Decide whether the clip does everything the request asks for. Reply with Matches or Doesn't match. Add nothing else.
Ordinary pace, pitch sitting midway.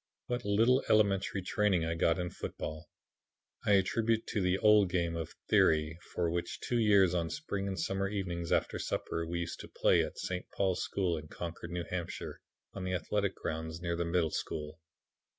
Doesn't match